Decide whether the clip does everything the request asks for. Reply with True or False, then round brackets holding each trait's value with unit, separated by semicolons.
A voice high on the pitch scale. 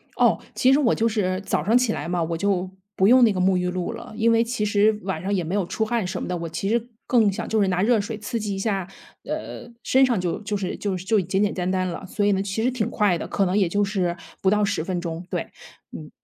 True (200 Hz)